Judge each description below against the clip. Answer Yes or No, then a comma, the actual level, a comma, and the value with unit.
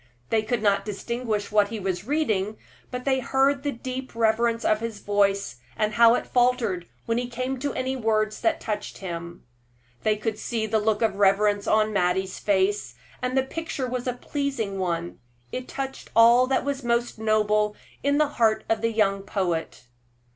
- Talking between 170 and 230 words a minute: Yes, average, 180 wpm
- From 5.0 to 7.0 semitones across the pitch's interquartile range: No, average, 3.7 semitones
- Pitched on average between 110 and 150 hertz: No, high, 220 Hz